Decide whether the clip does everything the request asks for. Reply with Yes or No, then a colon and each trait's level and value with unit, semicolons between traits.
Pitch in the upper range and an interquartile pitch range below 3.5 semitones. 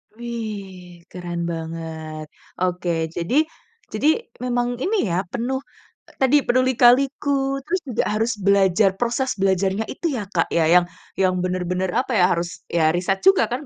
No: high, 195 Hz; wide, 5.6 semitones